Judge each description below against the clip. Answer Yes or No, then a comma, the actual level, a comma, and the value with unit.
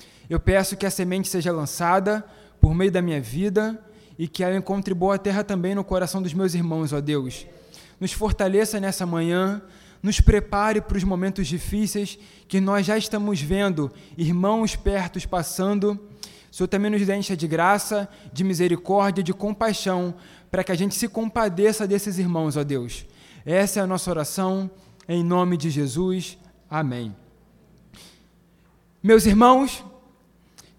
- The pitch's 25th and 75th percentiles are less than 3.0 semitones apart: Yes, narrow, 2.5 semitones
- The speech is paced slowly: No, average, 150 wpm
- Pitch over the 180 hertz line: Yes, high, 190 Hz